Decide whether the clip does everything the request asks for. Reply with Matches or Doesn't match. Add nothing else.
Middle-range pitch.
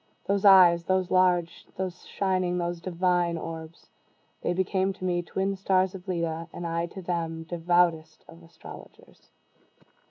Matches